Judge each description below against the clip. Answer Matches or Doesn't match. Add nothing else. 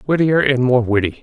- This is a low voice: Matches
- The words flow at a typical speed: Matches